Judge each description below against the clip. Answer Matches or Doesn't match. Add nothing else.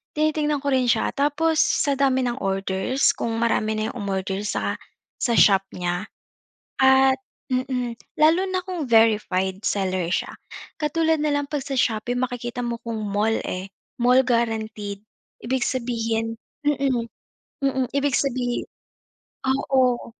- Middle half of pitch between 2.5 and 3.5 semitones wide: Doesn't match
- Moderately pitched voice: Doesn't match